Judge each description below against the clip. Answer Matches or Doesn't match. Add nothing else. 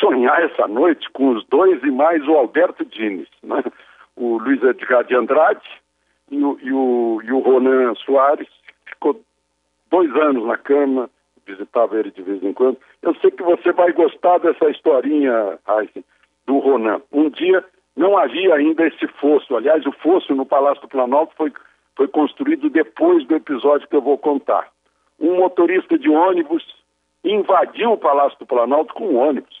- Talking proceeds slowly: Doesn't match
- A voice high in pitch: Doesn't match